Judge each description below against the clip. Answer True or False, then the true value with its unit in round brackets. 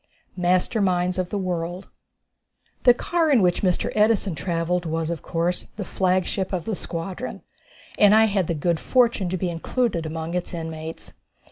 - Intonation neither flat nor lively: True (3.3 semitones)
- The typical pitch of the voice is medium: True (180 Hz)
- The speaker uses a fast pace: False (165 wpm)